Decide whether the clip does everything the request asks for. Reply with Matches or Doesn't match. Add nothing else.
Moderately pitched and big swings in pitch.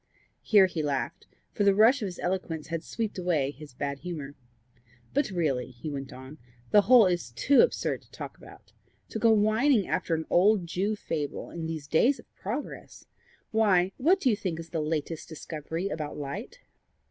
Matches